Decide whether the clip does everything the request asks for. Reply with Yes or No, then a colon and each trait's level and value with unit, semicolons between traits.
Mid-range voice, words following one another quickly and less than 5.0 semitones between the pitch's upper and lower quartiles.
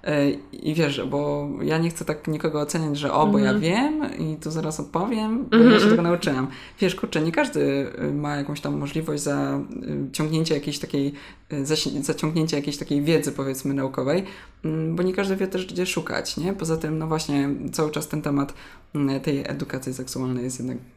Yes: medium, 155 Hz; fast, 170 wpm; average, 3.3 semitones